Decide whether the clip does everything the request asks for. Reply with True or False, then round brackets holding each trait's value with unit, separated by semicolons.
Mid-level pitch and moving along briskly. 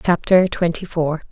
False (170 Hz; 135 wpm)